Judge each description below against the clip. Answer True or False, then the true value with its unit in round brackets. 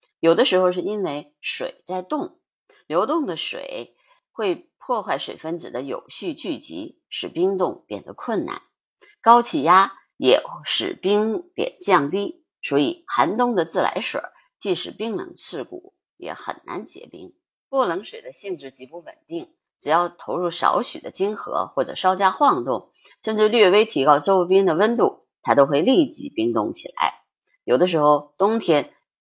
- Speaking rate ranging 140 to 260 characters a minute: True (230 characters per minute)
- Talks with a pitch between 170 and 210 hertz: False (235 Hz)